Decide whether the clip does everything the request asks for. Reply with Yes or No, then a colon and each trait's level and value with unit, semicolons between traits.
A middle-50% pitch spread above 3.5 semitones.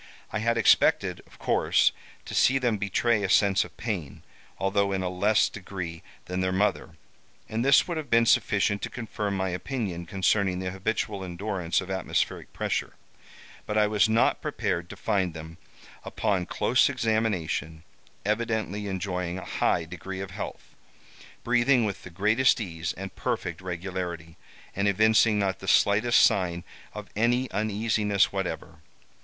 No: average, 3.1 semitones